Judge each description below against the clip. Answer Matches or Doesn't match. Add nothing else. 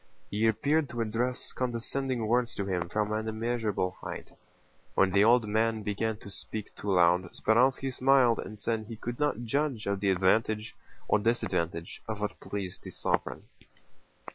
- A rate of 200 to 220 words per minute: Doesn't match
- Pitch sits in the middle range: Doesn't match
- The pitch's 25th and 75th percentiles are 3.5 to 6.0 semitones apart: Doesn't match